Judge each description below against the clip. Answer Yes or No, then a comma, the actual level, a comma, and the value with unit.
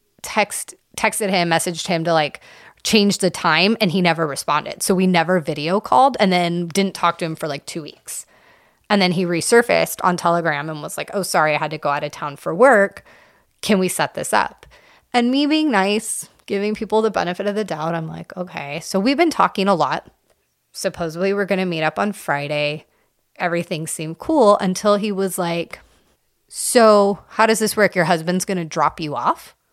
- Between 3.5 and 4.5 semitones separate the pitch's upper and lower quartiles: Yes, average, 3.9 semitones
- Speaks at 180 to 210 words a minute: Yes, fast, 205 wpm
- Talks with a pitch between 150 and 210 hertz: Yes, medium, 185 Hz